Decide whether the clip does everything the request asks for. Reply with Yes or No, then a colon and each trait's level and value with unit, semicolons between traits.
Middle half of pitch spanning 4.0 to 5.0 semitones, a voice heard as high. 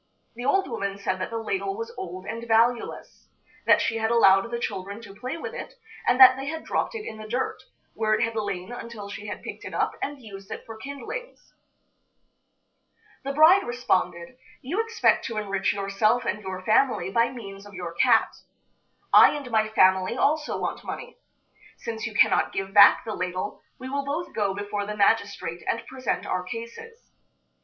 Yes: average, 4.7 semitones; high, 225 Hz